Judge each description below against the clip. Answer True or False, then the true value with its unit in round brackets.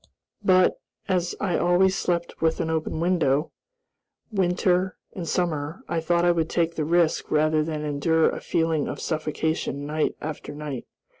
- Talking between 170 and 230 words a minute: False (155 wpm)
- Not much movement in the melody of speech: True (2.3 semitones)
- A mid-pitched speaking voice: True (165 Hz)